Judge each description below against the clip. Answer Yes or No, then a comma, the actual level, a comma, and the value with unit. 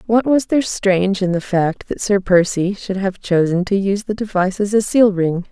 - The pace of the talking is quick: Yes, fast, 230 wpm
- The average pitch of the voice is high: Yes, high, 195 Hz